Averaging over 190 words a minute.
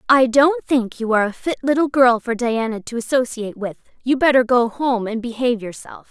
Yes: fast, 205 wpm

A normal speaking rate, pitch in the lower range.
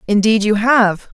No: average, 150 wpm; high, 215 Hz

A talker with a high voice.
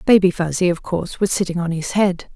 No: medium, 180 Hz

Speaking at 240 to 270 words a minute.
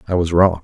No: fast, 285 wpm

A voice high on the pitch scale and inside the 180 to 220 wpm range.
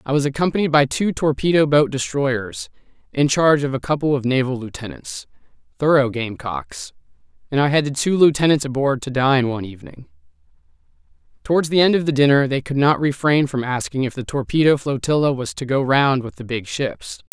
No: medium, 140 Hz; average, 185 wpm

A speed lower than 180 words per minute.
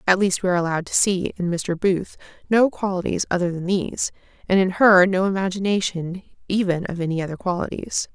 No: average, 185 wpm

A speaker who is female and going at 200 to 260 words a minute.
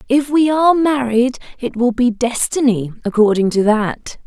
No: female; average, 155 wpm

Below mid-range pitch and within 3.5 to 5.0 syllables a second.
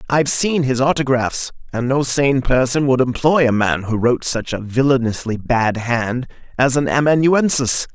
Yes: low, 130 Hz; 4.7 syllables/s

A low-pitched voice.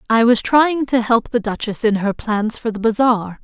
No: high, 230 Hz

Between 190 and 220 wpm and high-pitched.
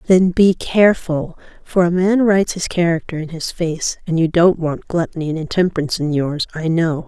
No: average, 195 wpm; medium, 170 Hz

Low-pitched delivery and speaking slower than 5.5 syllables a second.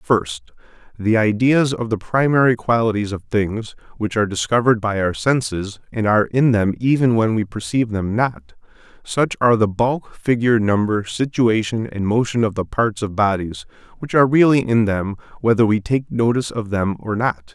Yes: low, 110 Hz; 5.1 syllables/s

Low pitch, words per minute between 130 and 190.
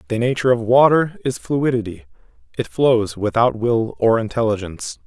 Yes: low, 120 Hz; average, 140 wpm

